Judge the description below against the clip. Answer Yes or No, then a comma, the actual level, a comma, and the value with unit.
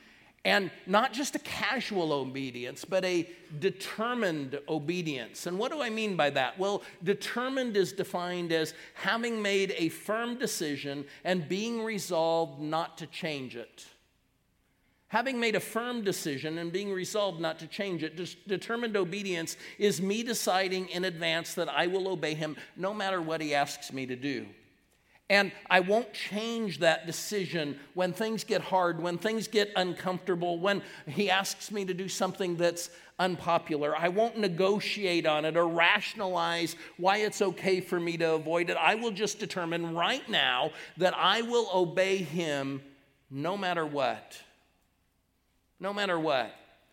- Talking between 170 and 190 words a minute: No, average, 155 wpm